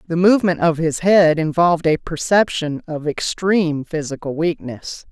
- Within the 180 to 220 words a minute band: No, average, 140 wpm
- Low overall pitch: No, medium, 165 Hz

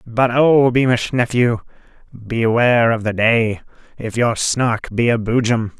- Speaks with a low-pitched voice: Yes, low, 115 Hz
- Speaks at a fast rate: No, average, 145 wpm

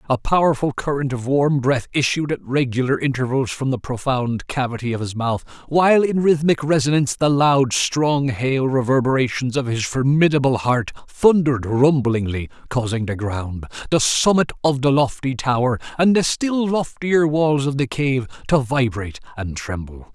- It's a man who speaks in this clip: Yes, male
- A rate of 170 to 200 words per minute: No, average, 160 wpm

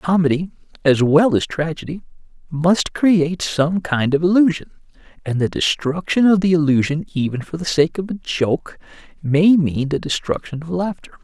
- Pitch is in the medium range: Yes, medium, 165 Hz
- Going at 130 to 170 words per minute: Yes, average, 160 wpm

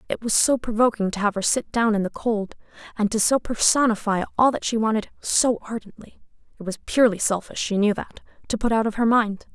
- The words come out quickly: Yes, fast, 210 wpm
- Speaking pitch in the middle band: No, high, 220 Hz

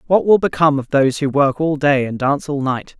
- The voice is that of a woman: No, male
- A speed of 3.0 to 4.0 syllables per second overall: No, 6.0 syllables/s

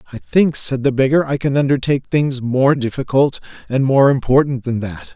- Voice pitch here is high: No, low, 135 Hz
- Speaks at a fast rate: No, average, 185 wpm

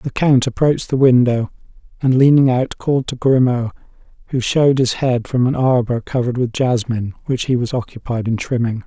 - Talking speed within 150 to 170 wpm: No, average, 185 wpm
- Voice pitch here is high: No, low, 125 Hz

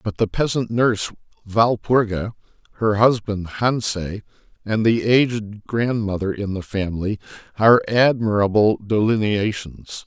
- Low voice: Yes, low, 110 Hz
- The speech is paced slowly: Yes, slow, 105 wpm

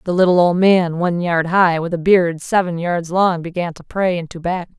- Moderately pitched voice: Yes, medium, 175 Hz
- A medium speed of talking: No, fast, 240 wpm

